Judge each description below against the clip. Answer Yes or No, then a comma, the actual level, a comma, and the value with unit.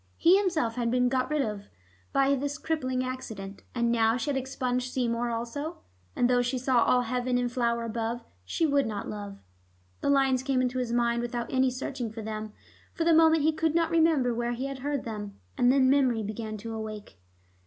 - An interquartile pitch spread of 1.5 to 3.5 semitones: Yes, average, 2.9 semitones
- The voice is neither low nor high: No, very high, 250 Hz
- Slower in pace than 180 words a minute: No, fast, 205 wpm